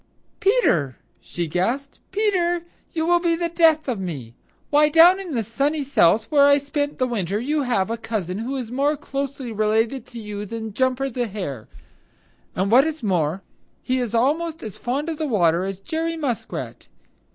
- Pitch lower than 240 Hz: No, very high, 255 Hz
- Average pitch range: No, wide, 6.4 semitones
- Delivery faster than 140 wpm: Yes, average, 180 wpm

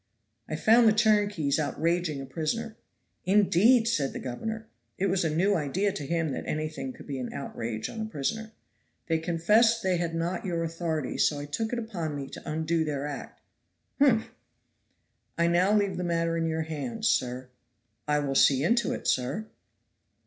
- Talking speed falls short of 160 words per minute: No, average, 175 wpm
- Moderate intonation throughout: No, wide, 5.9 semitones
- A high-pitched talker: No, medium, 170 Hz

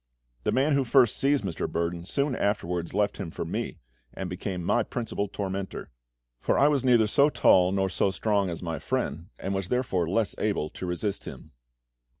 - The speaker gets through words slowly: No, average, 185 wpm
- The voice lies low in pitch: Yes, low, 100 Hz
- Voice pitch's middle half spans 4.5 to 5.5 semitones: Yes, average, 5.1 semitones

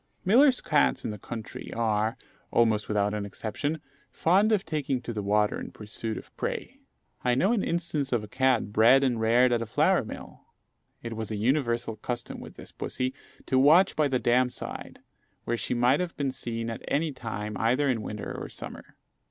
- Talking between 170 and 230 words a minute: Yes, average, 190 wpm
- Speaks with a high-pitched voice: No, low, 120 Hz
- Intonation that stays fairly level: No, average, 4.4 semitones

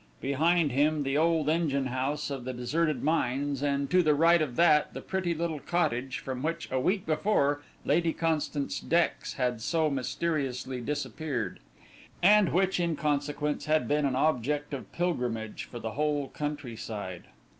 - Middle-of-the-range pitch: Yes, medium, 145 Hz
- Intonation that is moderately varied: Yes, average, 3.8 semitones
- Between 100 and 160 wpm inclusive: Yes, average, 155 wpm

